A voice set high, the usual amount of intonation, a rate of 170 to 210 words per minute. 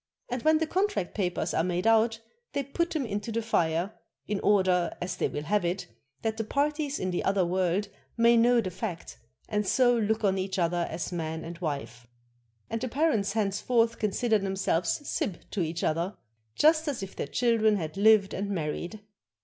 Yes: high, 205 Hz; average, 4.7 semitones; average, 190 wpm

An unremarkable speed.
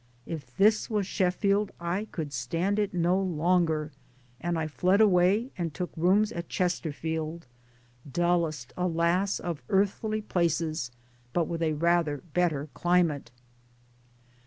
No: slow, 125 wpm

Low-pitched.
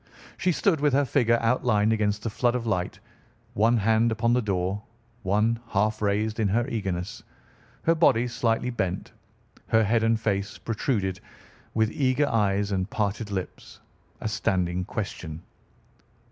Yes: low, 110 Hz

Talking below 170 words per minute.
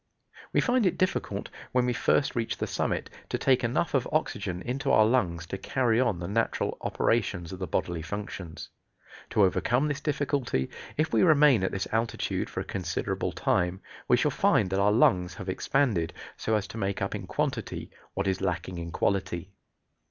No: average, 185 wpm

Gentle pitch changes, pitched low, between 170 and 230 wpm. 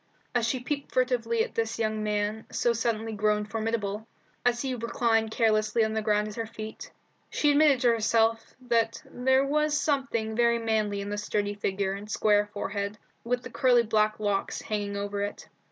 No: narrow, 2.2 semitones; high, 220 Hz; average, 180 wpm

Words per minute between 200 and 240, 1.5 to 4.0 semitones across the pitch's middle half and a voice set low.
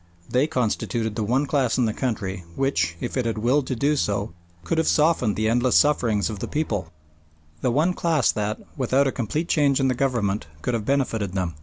No: fast, 205 wpm; average, 4.6 semitones; low, 125 Hz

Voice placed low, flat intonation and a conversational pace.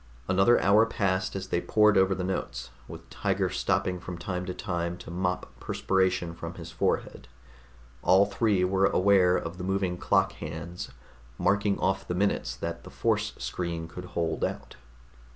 Yes: very low, 90 Hz; narrow, 1.8 semitones; average, 165 wpm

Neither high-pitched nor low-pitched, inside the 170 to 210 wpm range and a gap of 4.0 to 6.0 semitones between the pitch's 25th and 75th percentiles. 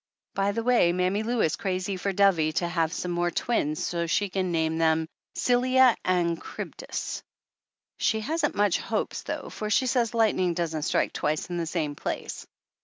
Yes: medium, 180 Hz; average, 180 wpm; average, 4.4 semitones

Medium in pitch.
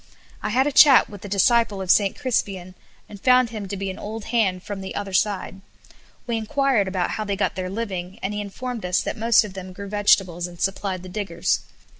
No: high, 200 Hz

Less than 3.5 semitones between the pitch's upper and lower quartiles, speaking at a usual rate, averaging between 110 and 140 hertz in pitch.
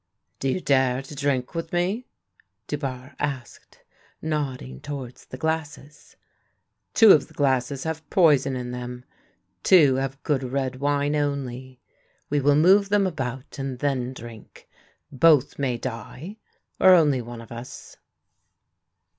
Yes: average, 3.1 semitones; average, 145 wpm; low, 135 Hz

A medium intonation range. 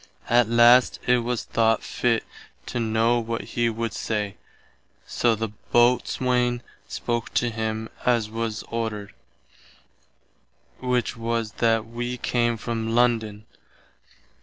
No: narrow, 1.3 semitones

